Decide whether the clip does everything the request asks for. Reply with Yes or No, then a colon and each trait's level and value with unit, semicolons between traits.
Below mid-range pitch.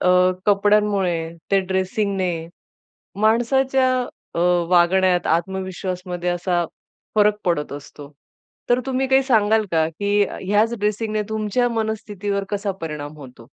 No: high, 200 Hz